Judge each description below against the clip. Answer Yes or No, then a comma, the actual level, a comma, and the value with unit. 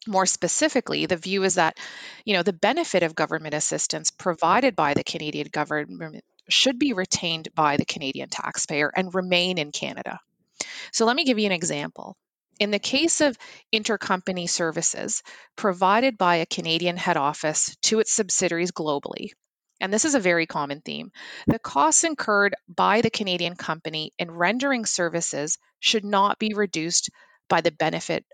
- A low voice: No, medium, 185 Hz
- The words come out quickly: No, average, 160 wpm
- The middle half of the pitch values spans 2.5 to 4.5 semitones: No, average, 5.0 semitones